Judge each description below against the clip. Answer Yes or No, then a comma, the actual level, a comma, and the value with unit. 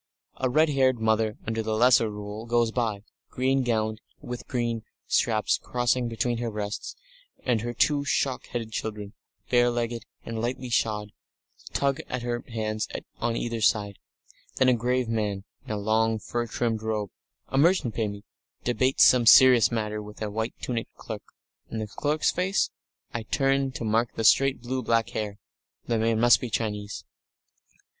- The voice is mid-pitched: No, low, 115 Hz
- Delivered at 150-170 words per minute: Yes, average, 165 wpm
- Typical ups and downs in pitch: No, narrow, 2.3 semitones